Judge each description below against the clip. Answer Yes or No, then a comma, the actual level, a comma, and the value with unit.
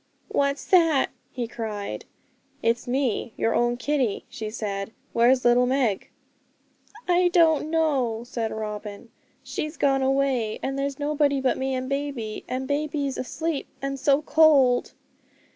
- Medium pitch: No, very high, 265 Hz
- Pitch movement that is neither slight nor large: Yes, average, 3.5 semitones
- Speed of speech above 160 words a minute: No, slow, 135 wpm